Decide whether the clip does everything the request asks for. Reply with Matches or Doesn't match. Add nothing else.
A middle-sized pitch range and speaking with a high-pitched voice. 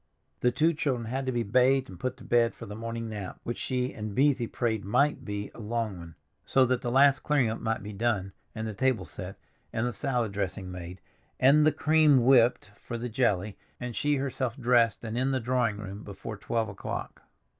Doesn't match